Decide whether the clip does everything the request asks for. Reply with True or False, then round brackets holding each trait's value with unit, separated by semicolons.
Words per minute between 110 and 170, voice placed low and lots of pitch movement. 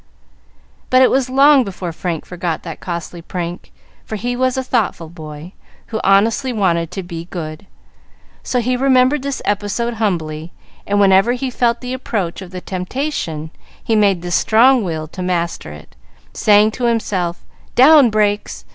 False (155 wpm; 205 Hz; 6.3 semitones)